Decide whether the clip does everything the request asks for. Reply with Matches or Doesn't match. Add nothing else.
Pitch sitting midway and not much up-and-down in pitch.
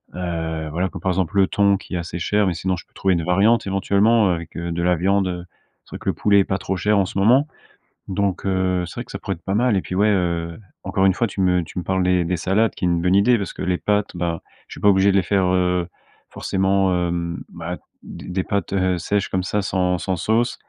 Doesn't match